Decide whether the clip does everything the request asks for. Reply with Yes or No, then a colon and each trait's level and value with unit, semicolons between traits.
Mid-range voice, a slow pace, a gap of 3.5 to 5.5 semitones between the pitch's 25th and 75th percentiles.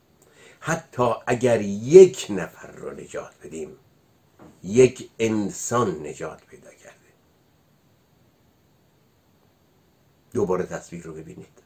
No: low, 120 Hz; slow, 80 wpm; average, 3.8 semitones